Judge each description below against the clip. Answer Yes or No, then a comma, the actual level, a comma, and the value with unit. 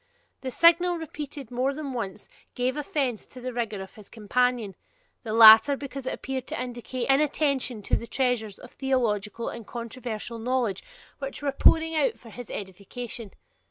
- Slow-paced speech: No, average, 160 wpm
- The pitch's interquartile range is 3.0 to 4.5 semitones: Yes, average, 3.6 semitones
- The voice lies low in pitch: No, very high, 250 Hz